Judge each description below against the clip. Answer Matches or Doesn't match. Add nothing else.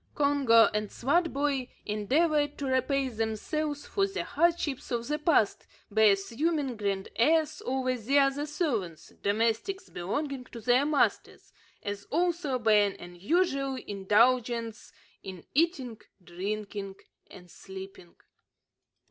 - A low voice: Doesn't match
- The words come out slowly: Matches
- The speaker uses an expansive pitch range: Matches